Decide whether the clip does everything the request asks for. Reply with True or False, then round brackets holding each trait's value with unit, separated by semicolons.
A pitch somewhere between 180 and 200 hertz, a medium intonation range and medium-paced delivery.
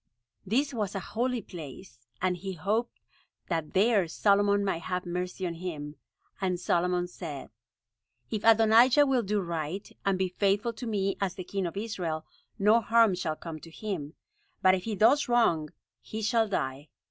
True (190 Hz; 4.2 semitones; 170 wpm)